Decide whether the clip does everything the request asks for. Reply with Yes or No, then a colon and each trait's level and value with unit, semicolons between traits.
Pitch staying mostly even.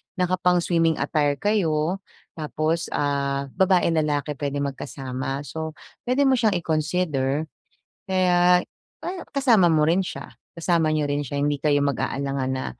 No: average, 3.9 semitones